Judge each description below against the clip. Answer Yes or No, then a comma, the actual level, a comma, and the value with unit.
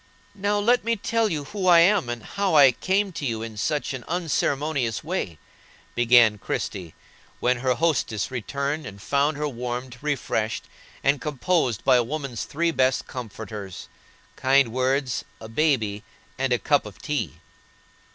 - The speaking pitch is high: No, low, 135 Hz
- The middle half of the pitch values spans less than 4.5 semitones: No, average, 4.8 semitones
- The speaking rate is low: No, average, 150 wpm